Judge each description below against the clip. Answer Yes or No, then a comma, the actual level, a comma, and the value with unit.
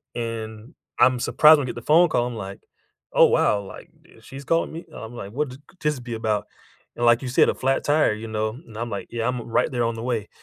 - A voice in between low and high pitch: No, low, 120 Hz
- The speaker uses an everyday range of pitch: Yes, average, 3.2 semitones